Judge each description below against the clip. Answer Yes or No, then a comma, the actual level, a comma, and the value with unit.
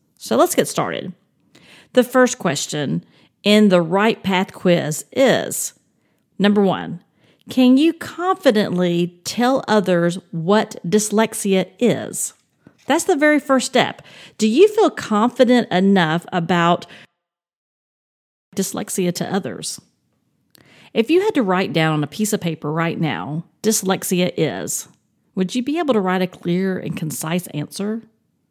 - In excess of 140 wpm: No, slow, 135 wpm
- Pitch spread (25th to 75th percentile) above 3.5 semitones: Yes, wide, 5.4 semitones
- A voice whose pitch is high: Yes, high, 195 Hz